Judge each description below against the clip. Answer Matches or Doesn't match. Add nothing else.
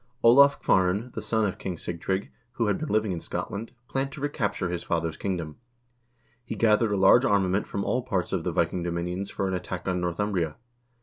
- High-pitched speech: Doesn't match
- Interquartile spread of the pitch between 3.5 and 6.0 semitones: Matches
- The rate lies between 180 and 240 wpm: Matches